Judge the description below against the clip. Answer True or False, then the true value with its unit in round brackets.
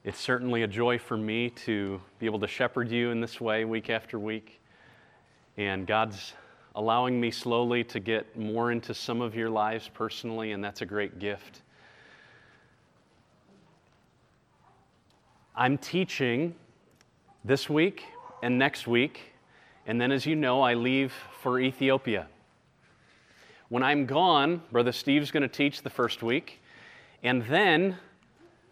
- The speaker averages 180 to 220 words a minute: False (140 wpm)